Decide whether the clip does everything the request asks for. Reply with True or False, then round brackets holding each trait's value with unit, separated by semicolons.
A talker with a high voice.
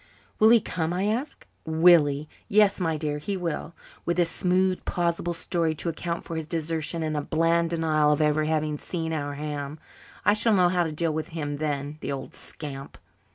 False (160 Hz)